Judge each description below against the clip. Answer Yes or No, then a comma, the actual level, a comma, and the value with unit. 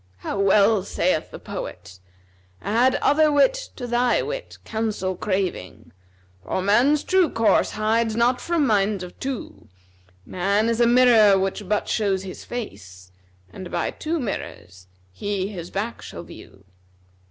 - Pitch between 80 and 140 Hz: No, high, 210 Hz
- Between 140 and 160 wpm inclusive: Yes, average, 150 wpm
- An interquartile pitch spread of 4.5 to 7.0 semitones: Yes, average, 4.8 semitones